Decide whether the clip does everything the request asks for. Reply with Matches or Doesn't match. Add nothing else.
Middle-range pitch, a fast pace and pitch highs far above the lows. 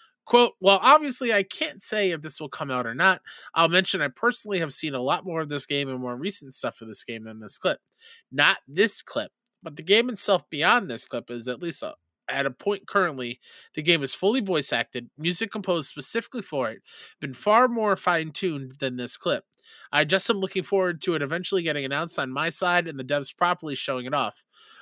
Matches